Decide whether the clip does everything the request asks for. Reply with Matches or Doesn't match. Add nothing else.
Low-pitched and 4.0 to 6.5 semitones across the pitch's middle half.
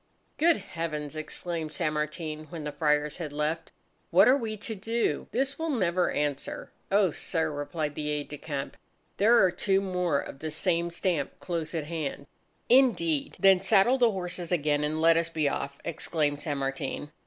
Doesn't match